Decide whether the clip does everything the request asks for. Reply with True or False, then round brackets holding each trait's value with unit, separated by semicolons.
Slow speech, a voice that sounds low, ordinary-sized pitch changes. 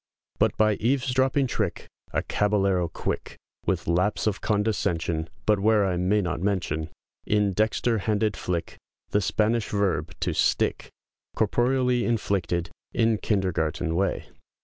True (125 wpm; 105 Hz; 3.6 semitones)